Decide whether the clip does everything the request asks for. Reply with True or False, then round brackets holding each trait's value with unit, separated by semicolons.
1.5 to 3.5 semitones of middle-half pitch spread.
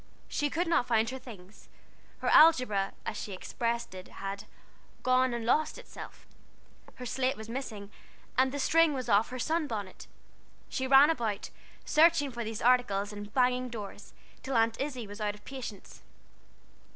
False (4.2 semitones)